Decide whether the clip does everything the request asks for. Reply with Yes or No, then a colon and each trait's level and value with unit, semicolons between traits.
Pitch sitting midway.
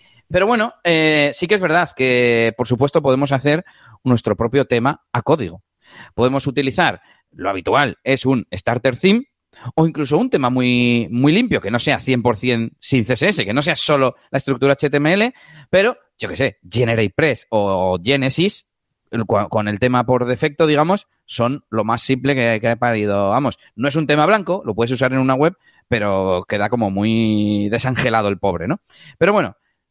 No: low, 130 Hz